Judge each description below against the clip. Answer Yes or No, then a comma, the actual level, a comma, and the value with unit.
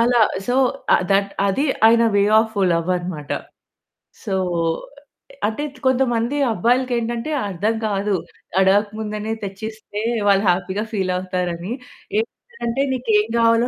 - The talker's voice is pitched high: Yes, high, 215 Hz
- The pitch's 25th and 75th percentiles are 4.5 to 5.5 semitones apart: No, average, 3.3 semitones